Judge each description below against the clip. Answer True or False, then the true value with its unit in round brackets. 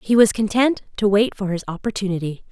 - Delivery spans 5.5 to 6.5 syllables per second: True (5.9 syllables/s)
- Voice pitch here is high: True (205 Hz)